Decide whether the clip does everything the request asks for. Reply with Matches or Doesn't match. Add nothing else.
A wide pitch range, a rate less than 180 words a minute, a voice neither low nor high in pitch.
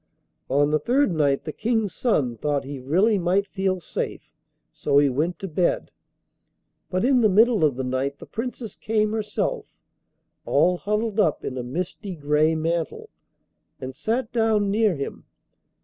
Matches